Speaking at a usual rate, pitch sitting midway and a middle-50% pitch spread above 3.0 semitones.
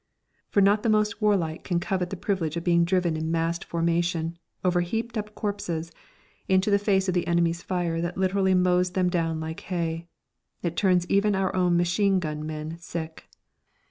No: average, 180 wpm; medium, 175 Hz; narrow, 2.5 semitones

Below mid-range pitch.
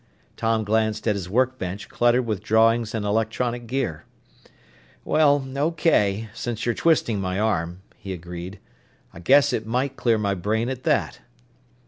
Yes: low, 110 Hz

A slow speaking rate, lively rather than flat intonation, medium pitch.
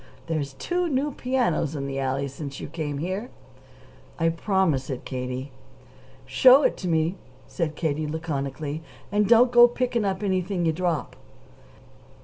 No: average, 150 wpm; wide, 6.5 semitones; medium, 165 Hz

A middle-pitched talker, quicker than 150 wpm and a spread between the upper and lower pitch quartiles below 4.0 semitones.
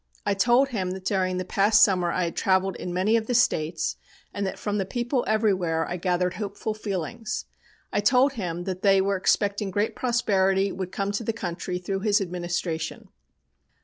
No: high, 195 Hz; average, 185 wpm; average, 2.9 semitones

